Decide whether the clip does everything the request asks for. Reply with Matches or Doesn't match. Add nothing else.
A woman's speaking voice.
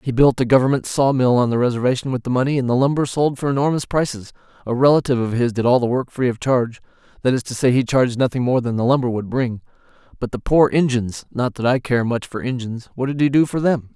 Doesn't match